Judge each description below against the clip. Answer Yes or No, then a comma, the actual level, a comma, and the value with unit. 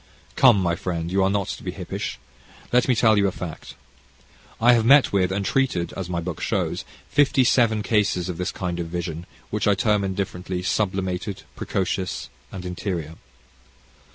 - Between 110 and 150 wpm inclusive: No, average, 175 wpm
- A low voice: Yes, very low, 95 Hz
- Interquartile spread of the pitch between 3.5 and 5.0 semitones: No, average, 3.0 semitones